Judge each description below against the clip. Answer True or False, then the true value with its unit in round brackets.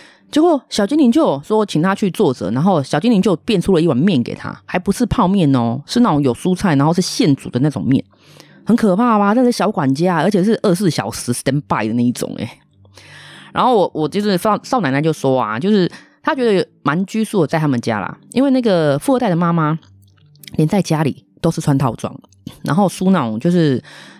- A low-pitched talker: False (175 Hz)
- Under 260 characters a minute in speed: False (320 characters per minute)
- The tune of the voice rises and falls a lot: True (6.6 semitones)